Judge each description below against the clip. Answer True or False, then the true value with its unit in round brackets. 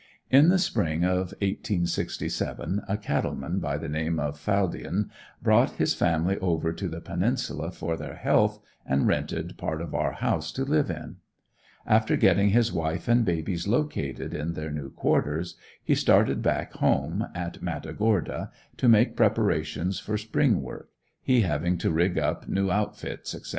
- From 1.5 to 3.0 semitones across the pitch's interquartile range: False (4.8 semitones)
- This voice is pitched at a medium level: False (90 Hz)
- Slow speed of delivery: False (160 wpm)